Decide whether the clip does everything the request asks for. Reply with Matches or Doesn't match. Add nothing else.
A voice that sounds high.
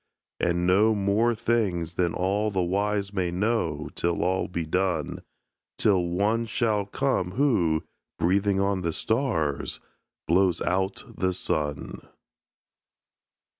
Doesn't match